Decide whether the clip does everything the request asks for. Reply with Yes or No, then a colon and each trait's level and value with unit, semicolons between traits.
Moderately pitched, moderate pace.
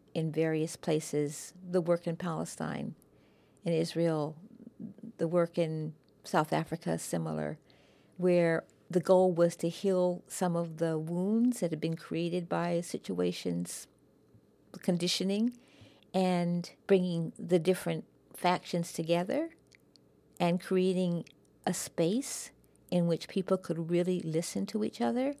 No: medium, 175 Hz; slow, 120 wpm